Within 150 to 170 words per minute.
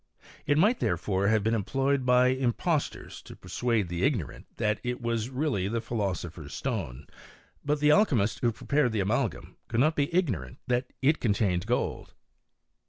Yes: average, 165 wpm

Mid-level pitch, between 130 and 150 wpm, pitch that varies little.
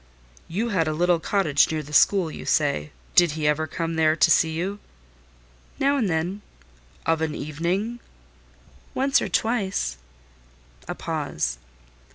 No: medium, 165 Hz; average, 145 wpm; average, 4.3 semitones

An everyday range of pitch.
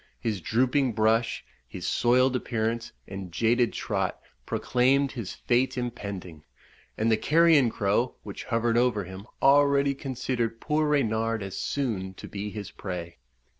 Yes: average, 4.2 semitones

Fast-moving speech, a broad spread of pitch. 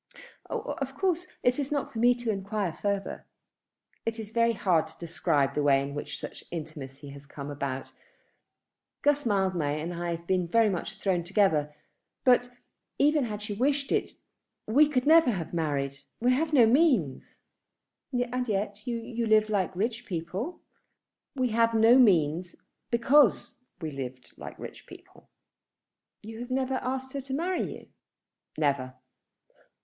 No: average, 155 wpm; wide, 7.4 semitones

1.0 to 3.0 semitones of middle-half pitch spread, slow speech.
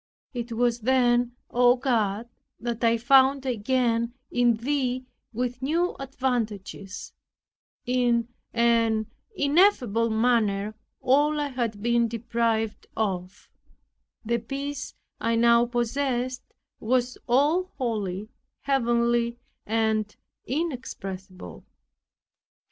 Yes: narrow, 2.4 semitones; slow, 90 wpm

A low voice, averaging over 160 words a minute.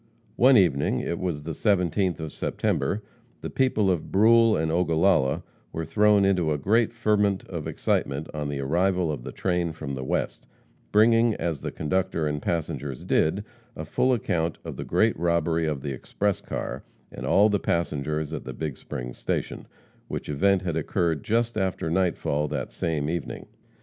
Yes: very low, 85 Hz; average, 170 wpm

